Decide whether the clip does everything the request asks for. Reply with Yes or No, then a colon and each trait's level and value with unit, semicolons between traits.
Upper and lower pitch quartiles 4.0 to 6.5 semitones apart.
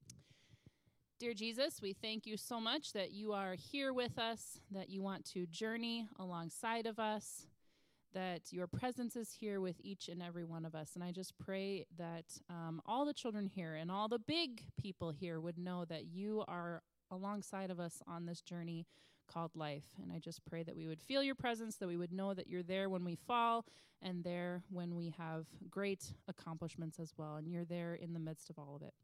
Yes: average, 4.3 semitones